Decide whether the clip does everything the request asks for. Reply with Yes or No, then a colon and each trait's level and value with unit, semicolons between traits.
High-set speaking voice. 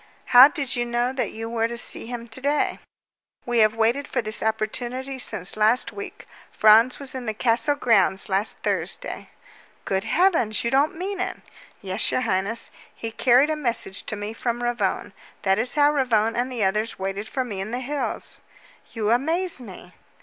Yes: high, 235 Hz